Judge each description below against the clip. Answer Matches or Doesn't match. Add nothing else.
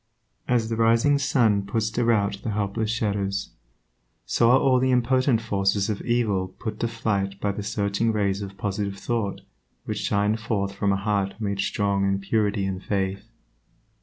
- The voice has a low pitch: Matches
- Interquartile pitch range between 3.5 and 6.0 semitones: Doesn't match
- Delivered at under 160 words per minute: Doesn't match